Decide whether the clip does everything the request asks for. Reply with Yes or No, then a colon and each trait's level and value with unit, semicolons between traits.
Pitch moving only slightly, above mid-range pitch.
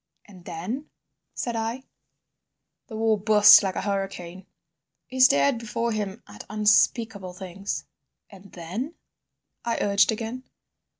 No: average, 3.2 semitones; high, 210 Hz